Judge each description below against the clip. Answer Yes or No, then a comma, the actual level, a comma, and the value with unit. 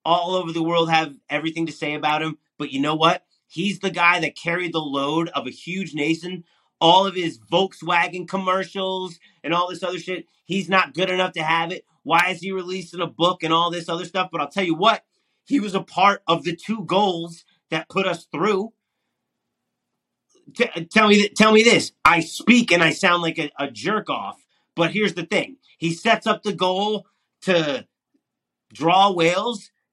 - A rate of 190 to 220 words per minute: Yes, average, 200 wpm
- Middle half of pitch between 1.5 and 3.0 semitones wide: Yes, average, 2.7 semitones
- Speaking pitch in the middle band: Yes, medium, 175 Hz